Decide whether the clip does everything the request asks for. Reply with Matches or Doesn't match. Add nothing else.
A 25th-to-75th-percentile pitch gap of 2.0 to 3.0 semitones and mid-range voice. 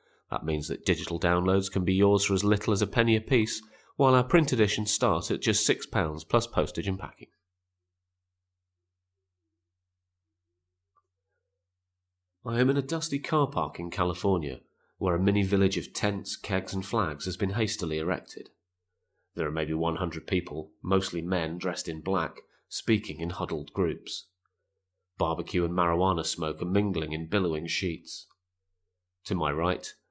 Doesn't match